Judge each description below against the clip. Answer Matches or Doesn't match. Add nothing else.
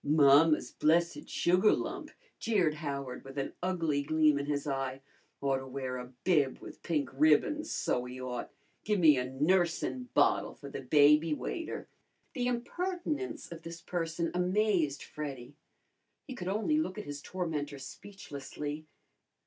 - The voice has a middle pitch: Matches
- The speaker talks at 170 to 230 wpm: Doesn't match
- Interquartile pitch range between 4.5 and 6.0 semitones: Matches